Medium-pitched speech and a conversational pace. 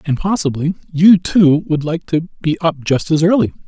Yes: medium, 160 Hz; average, 165 wpm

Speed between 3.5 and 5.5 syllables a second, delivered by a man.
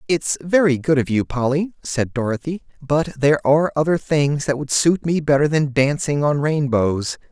Yes: 4.8 syllables/s; male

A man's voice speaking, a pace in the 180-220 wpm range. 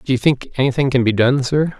No: male; fast, 300 wpm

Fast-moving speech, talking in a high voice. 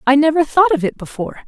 Yes: fast, 245 wpm; very high, 285 Hz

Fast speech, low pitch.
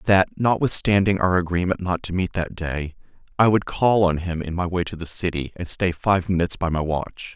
Yes: fast, 220 wpm; very low, 90 Hz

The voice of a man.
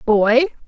No: female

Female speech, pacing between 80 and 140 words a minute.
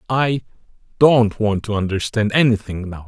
No: male; slow, 135 wpm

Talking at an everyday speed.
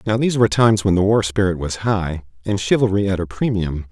No: fast, 230 wpm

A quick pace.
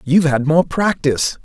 No: average, 165 wpm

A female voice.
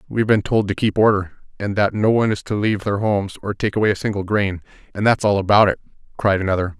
No: male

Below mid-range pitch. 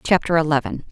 No: medium, 160 Hz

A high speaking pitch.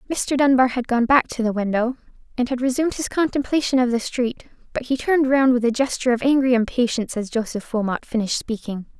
Yes: very high, 250 Hz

